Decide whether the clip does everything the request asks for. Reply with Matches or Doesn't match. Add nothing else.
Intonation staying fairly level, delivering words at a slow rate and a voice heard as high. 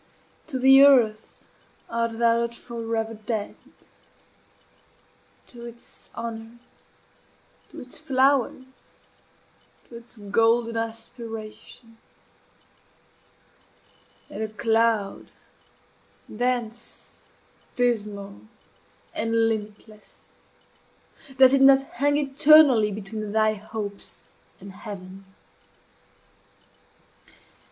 Matches